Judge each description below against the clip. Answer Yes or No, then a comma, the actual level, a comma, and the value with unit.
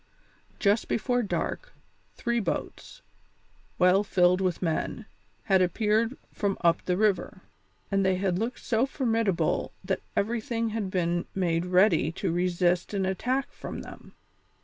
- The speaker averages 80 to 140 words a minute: Yes, slow, 135 wpm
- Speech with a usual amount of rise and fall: Yes, average, 4.0 semitones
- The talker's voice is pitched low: No, high, 195 Hz